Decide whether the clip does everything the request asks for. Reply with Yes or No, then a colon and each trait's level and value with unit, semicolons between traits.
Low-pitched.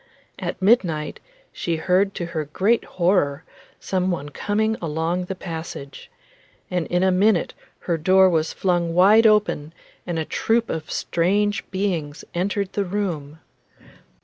No: medium, 180 Hz